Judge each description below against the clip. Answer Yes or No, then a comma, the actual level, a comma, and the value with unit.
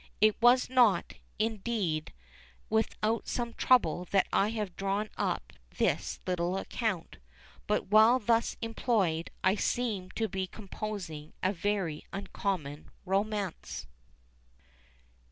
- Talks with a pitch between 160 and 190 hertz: No, high, 205 Hz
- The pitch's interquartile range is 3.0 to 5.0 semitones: Yes, average, 3.4 semitones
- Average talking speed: No, slow, 110 wpm